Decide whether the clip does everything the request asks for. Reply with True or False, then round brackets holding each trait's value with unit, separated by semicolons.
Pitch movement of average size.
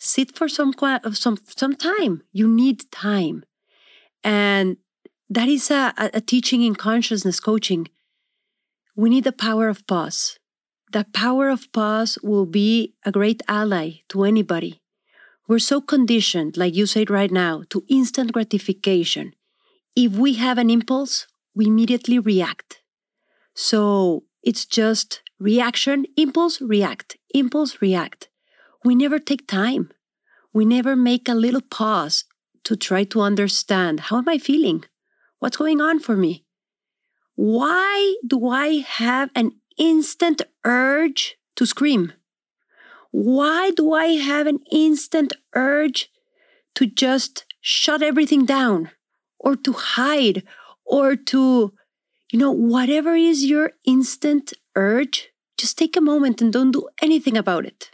False (5.7 semitones)